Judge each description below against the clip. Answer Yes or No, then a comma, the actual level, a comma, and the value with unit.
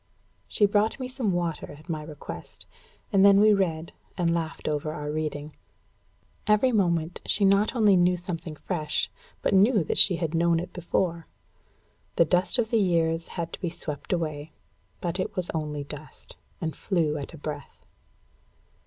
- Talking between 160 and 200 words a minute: Yes, average, 170 wpm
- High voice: No, medium, 170 Hz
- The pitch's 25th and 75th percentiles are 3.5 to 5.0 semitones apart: Yes, average, 3.8 semitones